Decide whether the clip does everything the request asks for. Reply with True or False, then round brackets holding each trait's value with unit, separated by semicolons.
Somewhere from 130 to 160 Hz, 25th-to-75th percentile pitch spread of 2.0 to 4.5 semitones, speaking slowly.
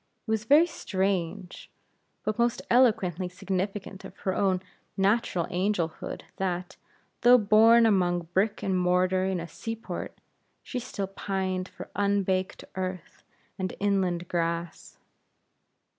False (190 Hz; 2.5 semitones; 125 wpm)